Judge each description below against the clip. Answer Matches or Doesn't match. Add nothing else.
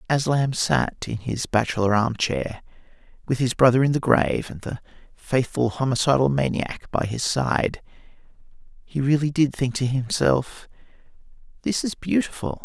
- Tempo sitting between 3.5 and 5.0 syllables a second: Matches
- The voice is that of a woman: Doesn't match